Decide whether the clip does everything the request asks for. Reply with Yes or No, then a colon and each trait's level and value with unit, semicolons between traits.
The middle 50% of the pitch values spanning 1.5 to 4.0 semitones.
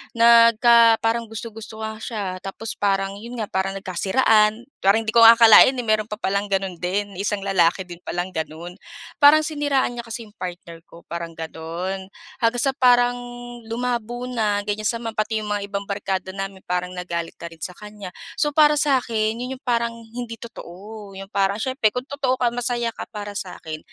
Yes: average, 3.4 semitones